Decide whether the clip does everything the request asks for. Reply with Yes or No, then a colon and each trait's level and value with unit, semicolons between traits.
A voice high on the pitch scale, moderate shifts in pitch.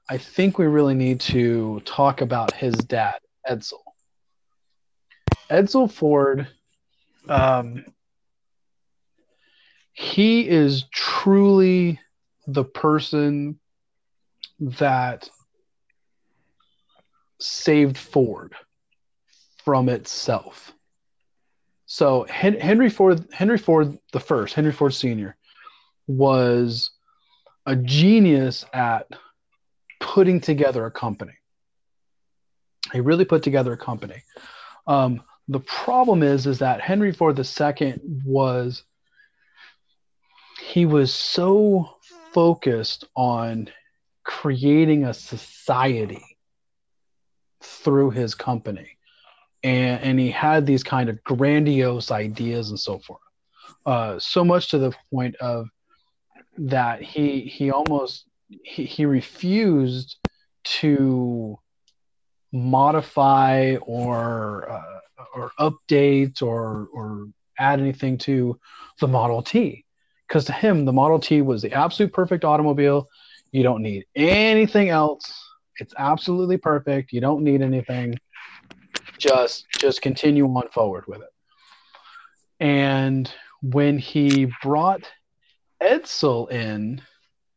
No: medium, 140 Hz; average, 4.2 semitones